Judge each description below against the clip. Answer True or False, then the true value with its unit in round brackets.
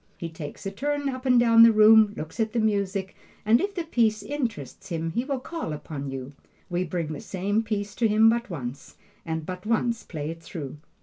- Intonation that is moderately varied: False (6.0 semitones)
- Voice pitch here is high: True (205 Hz)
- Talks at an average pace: False (210 wpm)